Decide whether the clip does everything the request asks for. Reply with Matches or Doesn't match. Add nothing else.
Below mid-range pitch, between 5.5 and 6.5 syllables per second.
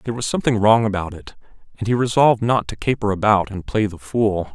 Matches